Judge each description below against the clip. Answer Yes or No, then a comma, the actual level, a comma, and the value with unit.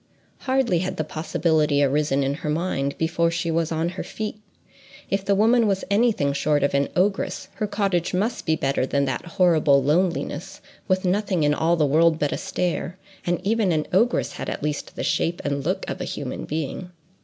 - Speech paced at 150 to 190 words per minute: No, average, 200 wpm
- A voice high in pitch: No, medium, 170 Hz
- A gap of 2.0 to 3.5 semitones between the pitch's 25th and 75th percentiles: No, average, 4.3 semitones